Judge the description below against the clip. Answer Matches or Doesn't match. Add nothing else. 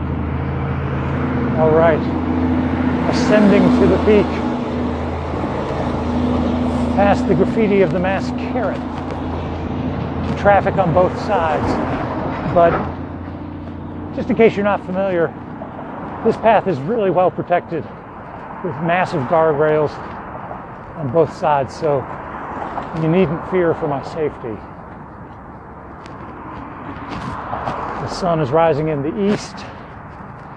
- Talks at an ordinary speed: Doesn't match